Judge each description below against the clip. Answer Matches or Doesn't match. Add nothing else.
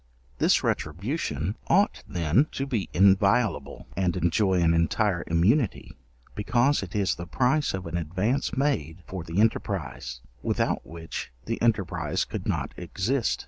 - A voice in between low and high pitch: Doesn't match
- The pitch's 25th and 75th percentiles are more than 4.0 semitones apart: Matches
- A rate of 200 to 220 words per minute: Doesn't match